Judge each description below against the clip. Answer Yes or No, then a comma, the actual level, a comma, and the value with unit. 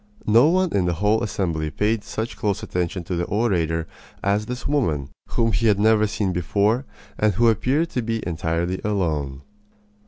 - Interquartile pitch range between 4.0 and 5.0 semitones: Yes, average, 4.6 semitones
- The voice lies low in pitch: Yes, low, 105 Hz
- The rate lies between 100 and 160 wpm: No, average, 180 wpm